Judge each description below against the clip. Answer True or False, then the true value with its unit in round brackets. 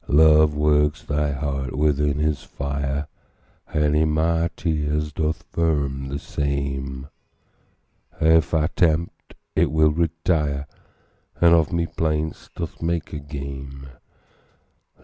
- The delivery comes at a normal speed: False (120 wpm)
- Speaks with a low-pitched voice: True (75 Hz)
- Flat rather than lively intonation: True (2.0 semitones)